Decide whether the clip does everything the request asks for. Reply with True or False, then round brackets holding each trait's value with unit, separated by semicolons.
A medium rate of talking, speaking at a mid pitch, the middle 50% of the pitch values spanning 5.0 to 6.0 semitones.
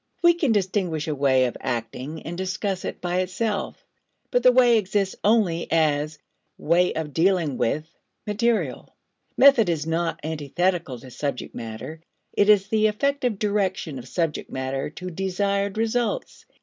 True (150 wpm; 180 Hz; 5.4 semitones)